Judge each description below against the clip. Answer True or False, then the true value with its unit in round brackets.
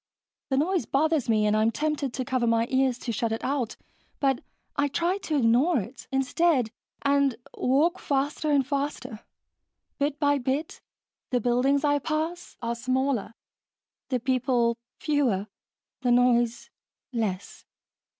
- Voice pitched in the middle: False (265 Hz)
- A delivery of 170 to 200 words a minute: False (140 wpm)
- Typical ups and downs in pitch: True (3.4 semitones)